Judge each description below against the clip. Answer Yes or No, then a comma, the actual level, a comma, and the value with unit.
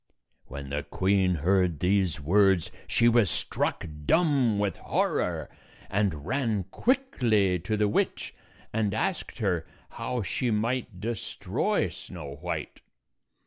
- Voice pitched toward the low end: Yes, low, 100 Hz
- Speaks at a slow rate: Yes, slow, 120 wpm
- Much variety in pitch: No, average, 4.4 semitones